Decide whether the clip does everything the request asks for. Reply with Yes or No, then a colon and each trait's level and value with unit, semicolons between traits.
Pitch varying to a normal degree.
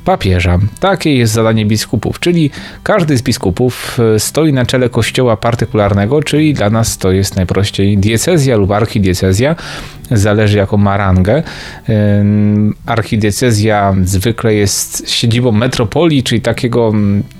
Yes: average, 3.5 semitones